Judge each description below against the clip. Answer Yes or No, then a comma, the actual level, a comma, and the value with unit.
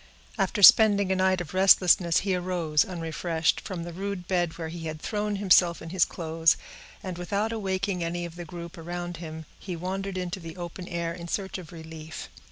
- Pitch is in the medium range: Yes, medium, 175 Hz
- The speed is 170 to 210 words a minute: Yes, average, 190 wpm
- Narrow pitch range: Yes, narrow, 2.1 semitones